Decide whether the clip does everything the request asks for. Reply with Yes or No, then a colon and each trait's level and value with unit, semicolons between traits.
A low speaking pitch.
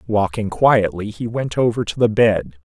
Yes: low, 105 Hz